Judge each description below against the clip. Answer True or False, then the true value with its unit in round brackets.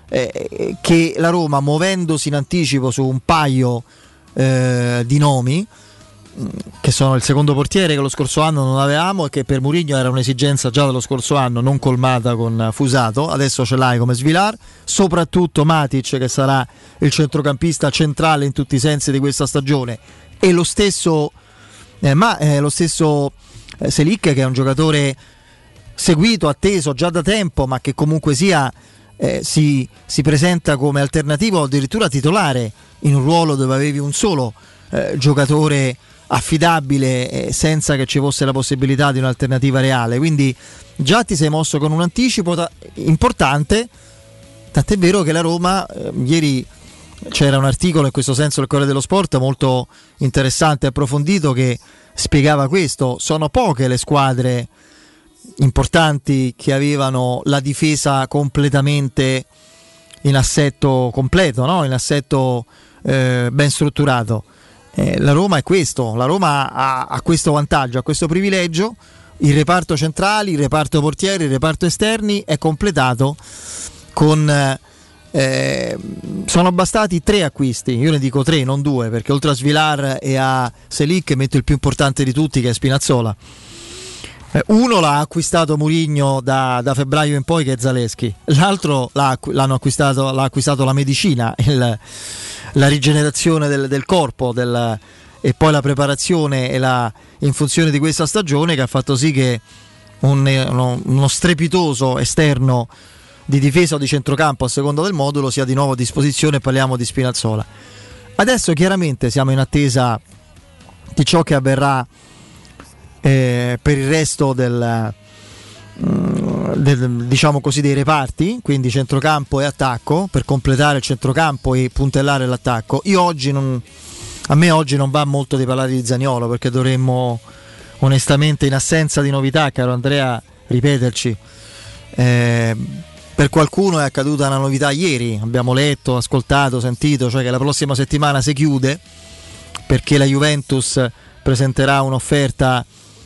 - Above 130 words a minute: True (150 wpm)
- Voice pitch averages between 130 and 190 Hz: True (140 Hz)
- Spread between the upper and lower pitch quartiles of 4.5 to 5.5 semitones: False (3.2 semitones)